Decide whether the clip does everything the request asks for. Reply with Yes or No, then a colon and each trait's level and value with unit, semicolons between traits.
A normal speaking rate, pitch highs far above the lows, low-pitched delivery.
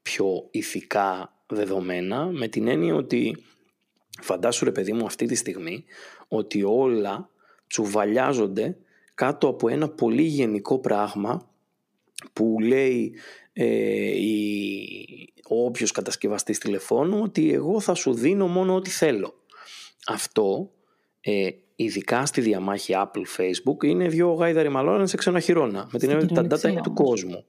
Yes: average, 130 wpm; wide, 8.8 semitones; low, 125 Hz